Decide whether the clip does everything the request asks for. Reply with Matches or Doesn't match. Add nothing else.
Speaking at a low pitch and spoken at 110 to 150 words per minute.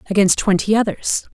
Doesn't match